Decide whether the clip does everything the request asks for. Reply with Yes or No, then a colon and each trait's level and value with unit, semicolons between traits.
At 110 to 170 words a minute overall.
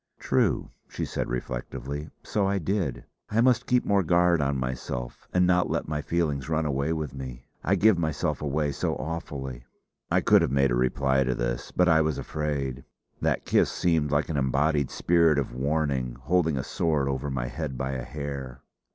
No: average, 185 wpm